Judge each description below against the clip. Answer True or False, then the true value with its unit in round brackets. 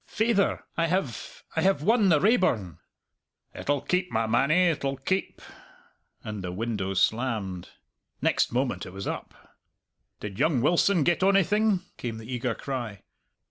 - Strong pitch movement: True (8.7 semitones)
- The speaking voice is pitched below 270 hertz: True (135 Hz)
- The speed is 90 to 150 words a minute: True (140 wpm)